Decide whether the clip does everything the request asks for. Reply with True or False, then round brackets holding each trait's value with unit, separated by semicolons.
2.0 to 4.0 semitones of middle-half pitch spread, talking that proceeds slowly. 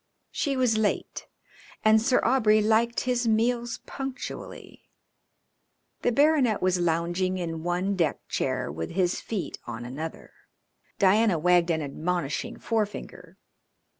False (5.5 semitones; 120 wpm)